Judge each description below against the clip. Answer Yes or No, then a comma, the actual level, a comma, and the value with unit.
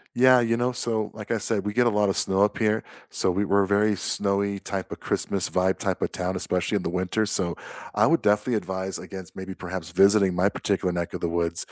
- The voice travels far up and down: No, narrow, 2.5 semitones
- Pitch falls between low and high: No, low, 100 Hz